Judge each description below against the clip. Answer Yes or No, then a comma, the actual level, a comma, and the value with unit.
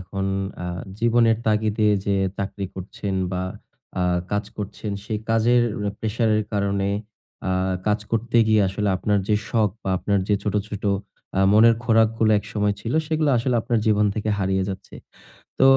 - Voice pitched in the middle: No, low, 105 Hz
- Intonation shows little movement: Yes, narrow, 2.1 semitones